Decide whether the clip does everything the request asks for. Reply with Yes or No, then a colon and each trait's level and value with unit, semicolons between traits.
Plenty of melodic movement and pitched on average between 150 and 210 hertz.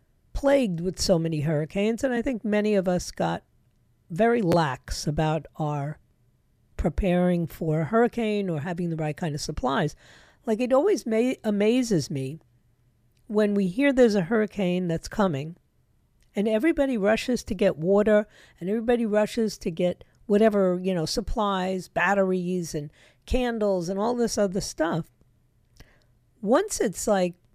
Yes: wide, 5.9 semitones; high, 190 Hz